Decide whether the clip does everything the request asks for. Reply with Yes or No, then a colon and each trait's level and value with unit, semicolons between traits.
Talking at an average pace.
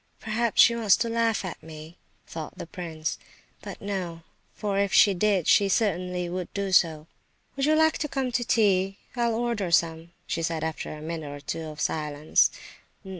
Yes: average, 175 wpm